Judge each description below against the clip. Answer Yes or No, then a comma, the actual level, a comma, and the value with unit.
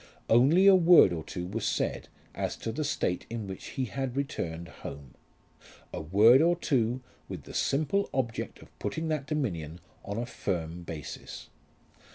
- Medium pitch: No, low, 115 Hz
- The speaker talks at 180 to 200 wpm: No, average, 165 wpm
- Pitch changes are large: Yes, wide, 8.6 semitones